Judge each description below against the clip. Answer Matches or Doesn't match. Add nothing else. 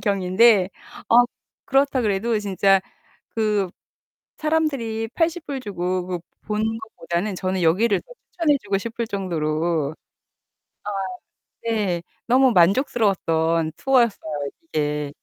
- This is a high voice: Matches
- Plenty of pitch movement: Doesn't match